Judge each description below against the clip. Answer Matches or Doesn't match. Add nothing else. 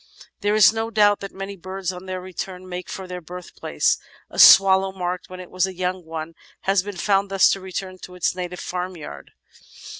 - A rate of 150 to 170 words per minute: Doesn't match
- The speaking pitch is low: Doesn't match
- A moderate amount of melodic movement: Doesn't match